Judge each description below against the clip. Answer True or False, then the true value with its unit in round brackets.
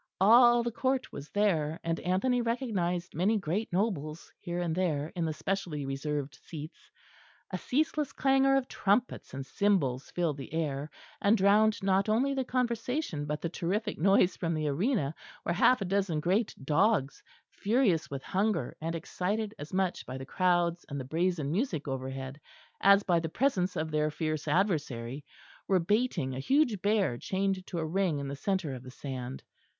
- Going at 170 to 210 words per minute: True (175 wpm)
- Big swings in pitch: True (5.7 semitones)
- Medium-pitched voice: True (180 Hz)